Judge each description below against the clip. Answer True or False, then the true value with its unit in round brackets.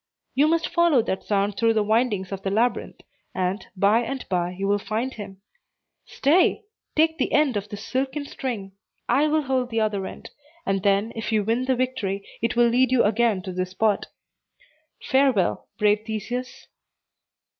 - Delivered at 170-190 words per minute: True (175 wpm)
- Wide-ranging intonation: False (4.5 semitones)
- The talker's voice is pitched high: True (225 Hz)